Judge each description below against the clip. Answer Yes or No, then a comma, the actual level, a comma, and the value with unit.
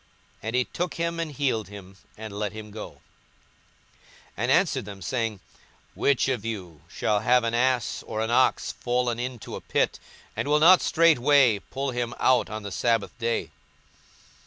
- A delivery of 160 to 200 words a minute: Yes, average, 170 wpm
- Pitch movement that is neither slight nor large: Yes, average, 3.3 semitones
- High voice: No, low, 120 Hz